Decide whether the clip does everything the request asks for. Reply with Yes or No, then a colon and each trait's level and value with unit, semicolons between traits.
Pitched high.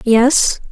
Yes: high, 245 Hz